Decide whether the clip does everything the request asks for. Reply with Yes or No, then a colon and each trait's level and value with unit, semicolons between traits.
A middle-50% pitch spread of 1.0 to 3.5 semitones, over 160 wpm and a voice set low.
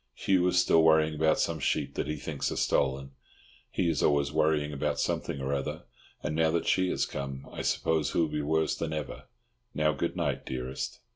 Yes: narrow, 2.4 semitones; average, 200 wpm; very low, 75 Hz